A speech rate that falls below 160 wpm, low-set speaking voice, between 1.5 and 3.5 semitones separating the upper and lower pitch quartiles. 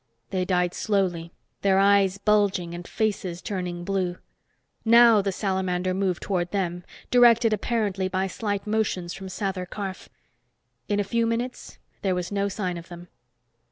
No: average, 150 wpm; high, 195 Hz; narrow, 2.5 semitones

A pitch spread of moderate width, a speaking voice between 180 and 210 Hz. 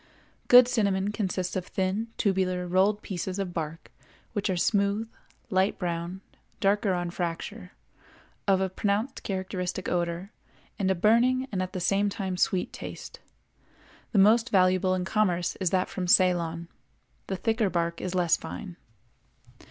No: narrow, 2.1 semitones; high, 190 Hz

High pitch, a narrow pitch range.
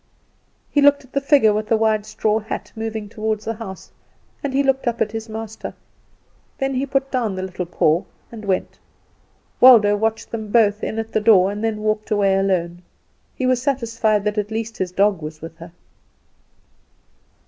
Yes: high, 220 Hz; narrow, 2.2 semitones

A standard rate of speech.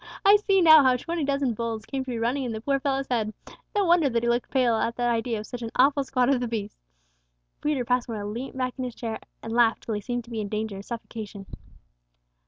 No: fast, 245 wpm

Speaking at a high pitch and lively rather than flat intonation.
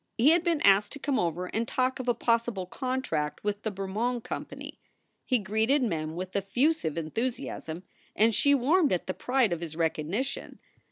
Yes: high, 220 Hz; wide, 6.2 semitones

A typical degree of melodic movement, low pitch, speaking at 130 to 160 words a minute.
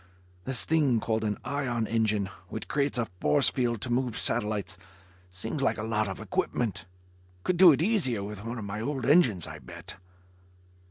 No: average, 4.3 semitones; low, 115 Hz; average, 175 wpm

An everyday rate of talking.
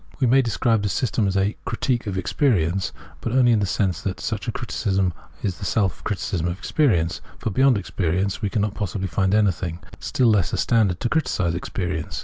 No: fast, 210 wpm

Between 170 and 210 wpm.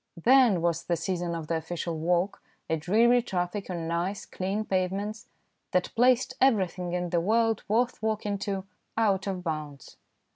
No: average, 155 wpm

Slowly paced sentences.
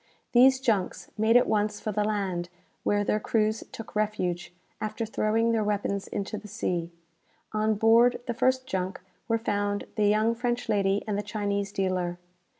No: average, 165 wpm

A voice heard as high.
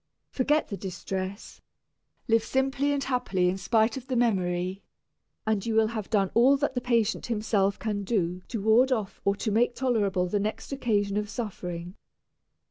Yes: high, 215 Hz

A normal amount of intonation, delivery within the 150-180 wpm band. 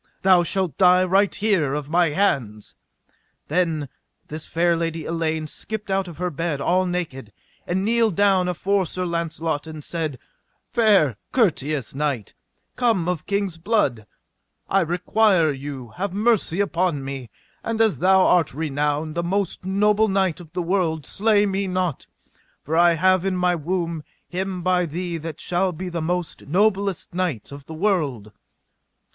Yes: average, 3.7 semitones; average, 155 wpm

